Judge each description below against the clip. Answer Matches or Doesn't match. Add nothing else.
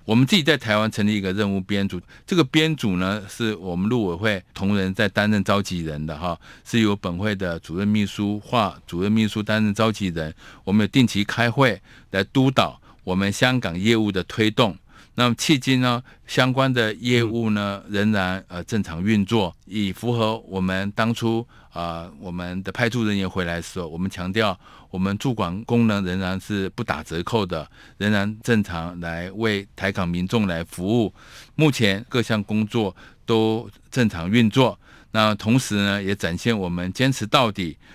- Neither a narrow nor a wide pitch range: Matches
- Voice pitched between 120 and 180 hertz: Doesn't match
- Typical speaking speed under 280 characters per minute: Matches